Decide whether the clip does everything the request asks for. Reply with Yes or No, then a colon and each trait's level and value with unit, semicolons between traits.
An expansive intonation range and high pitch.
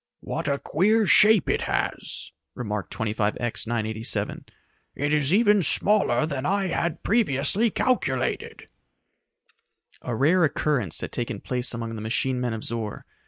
No: wide, 8.2 semitones; low, 135 Hz